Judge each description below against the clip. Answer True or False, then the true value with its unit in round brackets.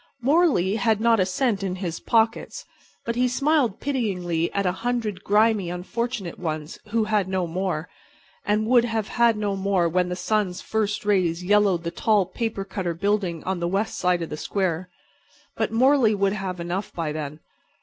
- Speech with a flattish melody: False (3.8 semitones)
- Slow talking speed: False (180 wpm)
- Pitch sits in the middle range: False (195 Hz)